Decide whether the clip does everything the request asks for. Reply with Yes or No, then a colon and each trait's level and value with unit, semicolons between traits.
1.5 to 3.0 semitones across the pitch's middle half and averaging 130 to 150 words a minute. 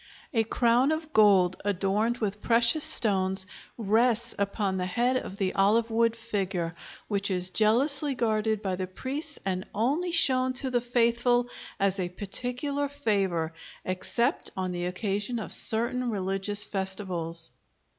No: average, 4.2 semitones; average, 140 wpm